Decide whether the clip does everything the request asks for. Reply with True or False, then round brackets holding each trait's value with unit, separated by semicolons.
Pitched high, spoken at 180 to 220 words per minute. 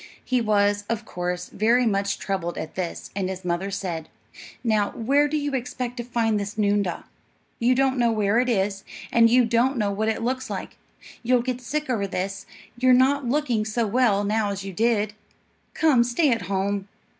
True (220 Hz; 190 wpm)